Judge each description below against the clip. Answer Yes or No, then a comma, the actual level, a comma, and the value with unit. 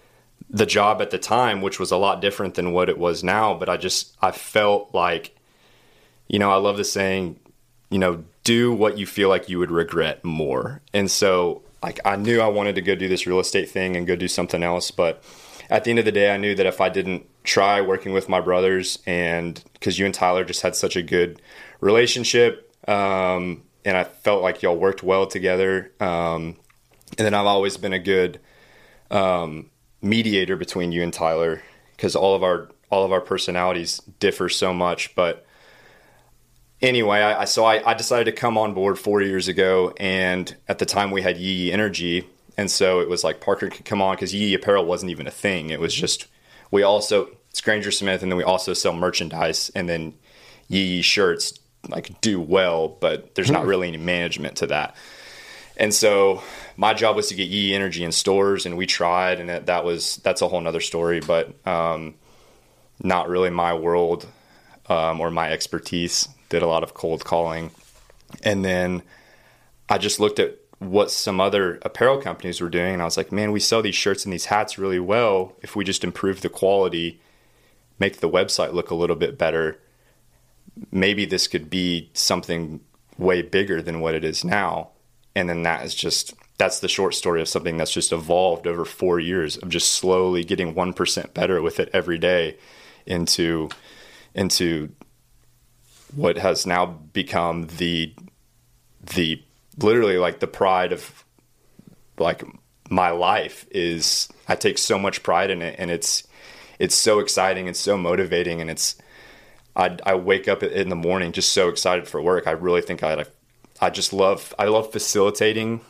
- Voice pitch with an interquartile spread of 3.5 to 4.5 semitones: No, average, 2.8 semitones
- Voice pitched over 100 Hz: No, very low, 95 Hz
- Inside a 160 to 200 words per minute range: Yes, average, 190 wpm